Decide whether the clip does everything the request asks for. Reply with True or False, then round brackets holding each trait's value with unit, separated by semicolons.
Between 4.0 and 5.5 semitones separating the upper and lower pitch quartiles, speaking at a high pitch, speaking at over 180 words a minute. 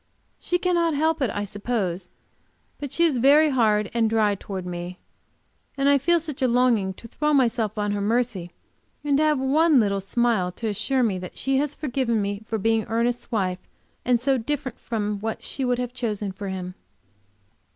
True (4.9 semitones; 235 Hz; 190 wpm)